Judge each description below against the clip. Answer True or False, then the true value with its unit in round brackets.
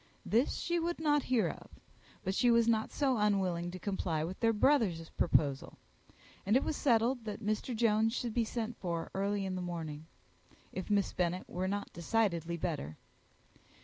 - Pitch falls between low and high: False (205 Hz)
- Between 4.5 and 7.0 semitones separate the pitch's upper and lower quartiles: True (4.9 semitones)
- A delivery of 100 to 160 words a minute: False (175 wpm)